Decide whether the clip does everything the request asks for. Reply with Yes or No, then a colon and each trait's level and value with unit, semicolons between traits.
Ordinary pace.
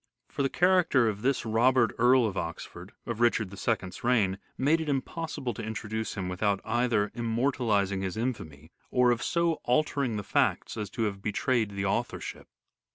Yes: average, 165 wpm